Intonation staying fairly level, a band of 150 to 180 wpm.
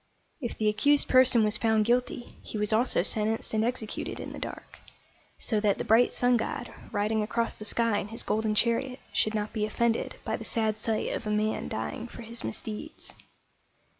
No: narrow, 1.8 semitones; average, 195 wpm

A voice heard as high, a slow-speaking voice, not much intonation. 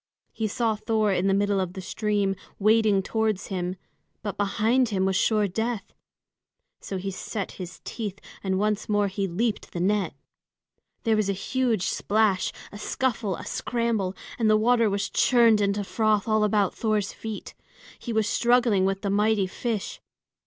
No: high, 210 Hz; average, 165 wpm; narrow, 2.2 semitones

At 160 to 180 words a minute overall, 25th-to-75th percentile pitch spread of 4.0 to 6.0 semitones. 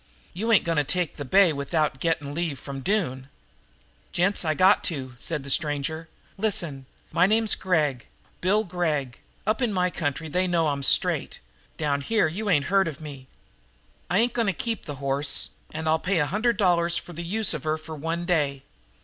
No: average, 190 wpm; average, 4.7 semitones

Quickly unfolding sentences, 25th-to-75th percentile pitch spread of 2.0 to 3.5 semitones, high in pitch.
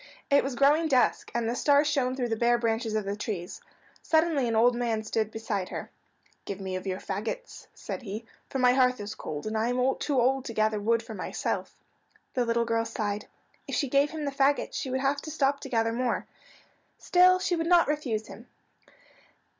No: fast, 210 wpm; average, 4.1 semitones; high, 240 Hz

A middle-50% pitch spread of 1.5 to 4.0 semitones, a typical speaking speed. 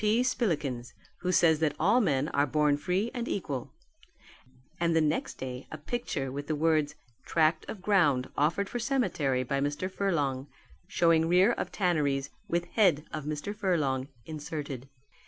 No: average, 4.6 semitones; average, 155 wpm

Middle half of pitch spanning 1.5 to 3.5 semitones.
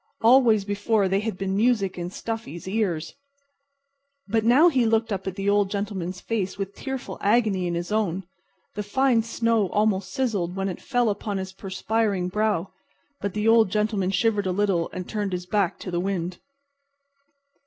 Yes: average, 2.9 semitones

